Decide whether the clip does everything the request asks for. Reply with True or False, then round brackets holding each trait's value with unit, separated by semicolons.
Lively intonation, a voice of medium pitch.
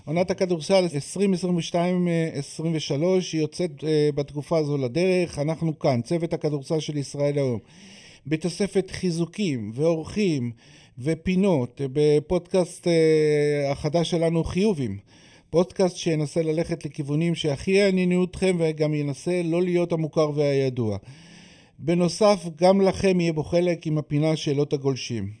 False (3.4 semitones; 160 Hz)